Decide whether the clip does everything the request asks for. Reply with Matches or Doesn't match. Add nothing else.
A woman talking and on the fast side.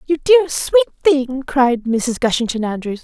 Doesn't match